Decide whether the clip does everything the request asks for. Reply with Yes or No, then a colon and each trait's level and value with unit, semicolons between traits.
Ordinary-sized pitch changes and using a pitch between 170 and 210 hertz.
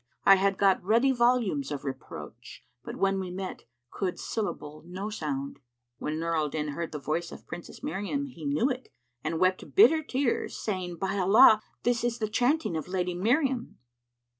No: wide, 6.4 semitones; high, 190 Hz